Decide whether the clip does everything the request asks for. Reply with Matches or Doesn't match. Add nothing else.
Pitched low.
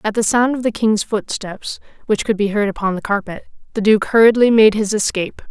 Doesn't match